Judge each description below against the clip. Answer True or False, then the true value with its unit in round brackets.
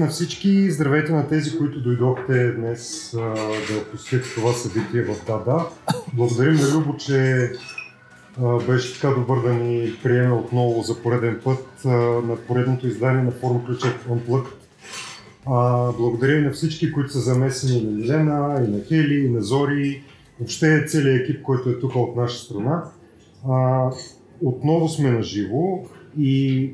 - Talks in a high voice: False (130 Hz)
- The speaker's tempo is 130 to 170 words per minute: True (160 wpm)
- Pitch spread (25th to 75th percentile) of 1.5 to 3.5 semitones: True (3.2 semitones)